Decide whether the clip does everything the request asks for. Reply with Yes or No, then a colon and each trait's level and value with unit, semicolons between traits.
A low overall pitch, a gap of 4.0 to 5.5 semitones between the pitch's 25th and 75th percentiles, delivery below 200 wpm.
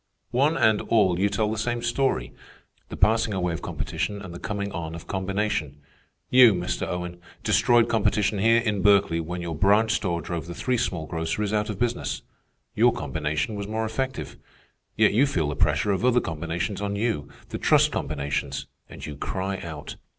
Yes: low, 100 Hz; average, 4.8 semitones; average, 180 wpm